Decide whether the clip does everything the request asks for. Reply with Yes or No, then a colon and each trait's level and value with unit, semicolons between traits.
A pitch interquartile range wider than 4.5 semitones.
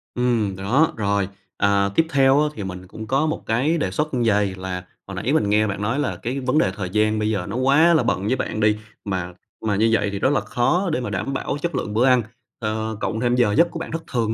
Yes: average, 4.9 semitones